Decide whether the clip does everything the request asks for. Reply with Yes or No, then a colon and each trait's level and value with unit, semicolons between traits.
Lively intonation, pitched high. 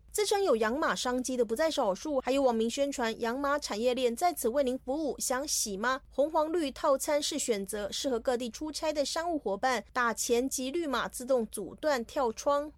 No: average, 3.7 semitones; very high, 260 Hz